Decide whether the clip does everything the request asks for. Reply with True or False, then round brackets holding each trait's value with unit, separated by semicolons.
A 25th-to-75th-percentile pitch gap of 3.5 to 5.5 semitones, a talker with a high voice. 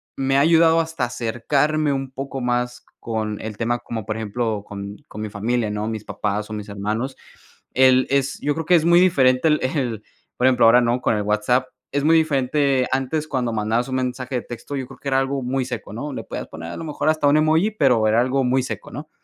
False (4.0 semitones; 130 Hz)